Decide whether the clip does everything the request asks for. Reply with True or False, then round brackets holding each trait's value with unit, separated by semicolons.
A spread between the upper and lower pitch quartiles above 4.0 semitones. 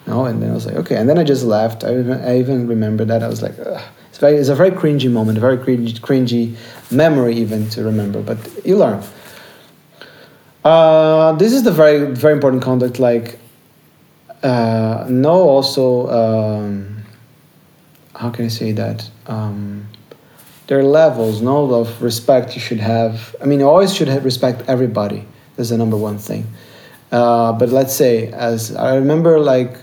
False (3.4 semitones)